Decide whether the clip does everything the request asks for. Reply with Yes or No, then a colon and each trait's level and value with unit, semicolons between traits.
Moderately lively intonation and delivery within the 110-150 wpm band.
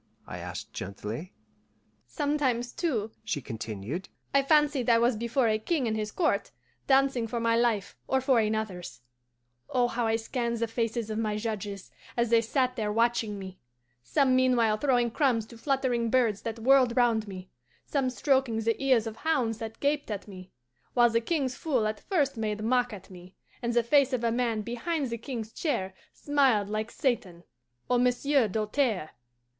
No: average, 3.3 semitones; average, 175 wpm